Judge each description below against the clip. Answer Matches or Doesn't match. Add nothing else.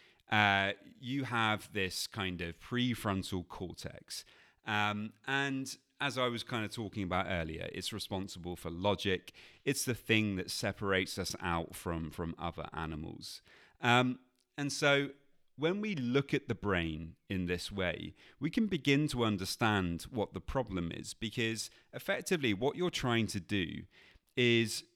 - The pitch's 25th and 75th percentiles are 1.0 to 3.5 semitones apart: Doesn't match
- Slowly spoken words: Doesn't match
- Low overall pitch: Matches